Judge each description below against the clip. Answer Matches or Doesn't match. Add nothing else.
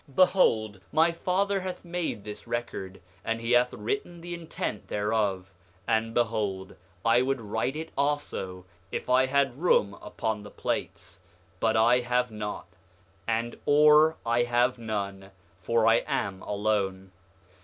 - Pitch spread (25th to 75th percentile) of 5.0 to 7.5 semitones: Matches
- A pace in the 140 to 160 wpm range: Matches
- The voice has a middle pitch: Doesn't match